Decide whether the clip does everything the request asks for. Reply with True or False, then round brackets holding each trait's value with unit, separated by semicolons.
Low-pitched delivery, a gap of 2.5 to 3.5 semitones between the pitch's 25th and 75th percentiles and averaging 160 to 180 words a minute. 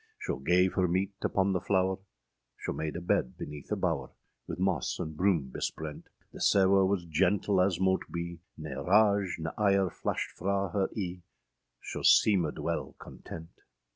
True (95 Hz; 2.8 semitones; 165 wpm)